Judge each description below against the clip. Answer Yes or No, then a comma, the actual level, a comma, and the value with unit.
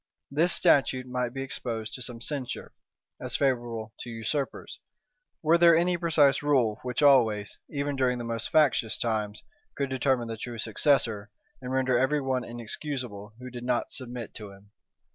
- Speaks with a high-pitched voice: No, low, 125 Hz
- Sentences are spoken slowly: No, average, 160 wpm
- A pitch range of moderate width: Yes, average, 3.4 semitones